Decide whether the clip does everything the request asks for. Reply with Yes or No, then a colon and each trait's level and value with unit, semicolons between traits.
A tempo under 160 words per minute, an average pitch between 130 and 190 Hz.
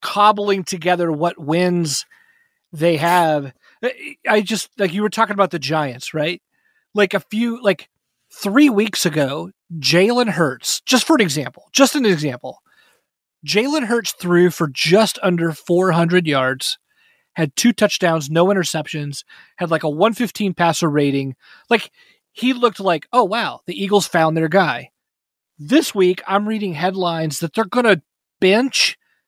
Yes: average, 150 wpm; medium, 185 Hz